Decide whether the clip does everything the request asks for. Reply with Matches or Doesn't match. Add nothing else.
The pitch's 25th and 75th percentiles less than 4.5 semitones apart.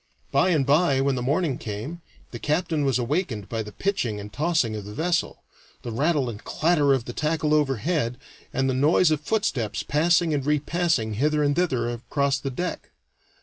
Doesn't match